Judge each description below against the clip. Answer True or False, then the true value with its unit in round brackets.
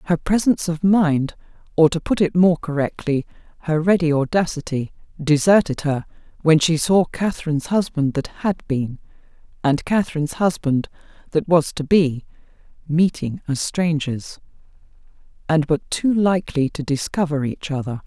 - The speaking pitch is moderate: True (160 Hz)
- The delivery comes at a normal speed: False (130 wpm)